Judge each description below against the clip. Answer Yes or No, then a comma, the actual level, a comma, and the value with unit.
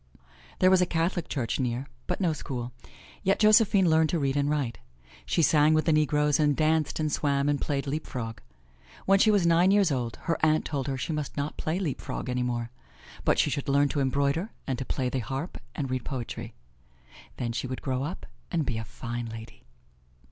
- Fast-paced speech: Yes, fast, 210 wpm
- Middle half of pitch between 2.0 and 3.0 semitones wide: No, average, 3.8 semitones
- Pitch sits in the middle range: Yes, medium, 145 Hz